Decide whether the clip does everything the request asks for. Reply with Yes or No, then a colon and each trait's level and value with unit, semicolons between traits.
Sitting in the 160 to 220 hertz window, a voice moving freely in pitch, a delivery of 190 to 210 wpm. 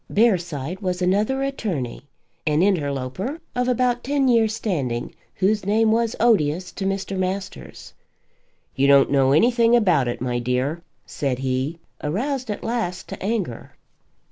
No: medium, 185 Hz; wide, 8.3 semitones; average, 140 wpm